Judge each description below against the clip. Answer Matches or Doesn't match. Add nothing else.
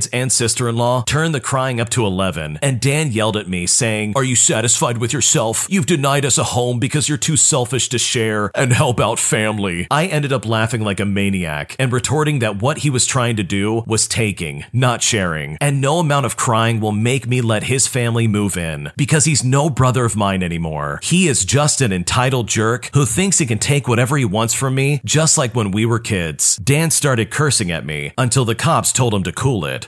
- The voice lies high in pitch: Doesn't match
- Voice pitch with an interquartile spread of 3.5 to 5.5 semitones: Matches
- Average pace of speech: Doesn't match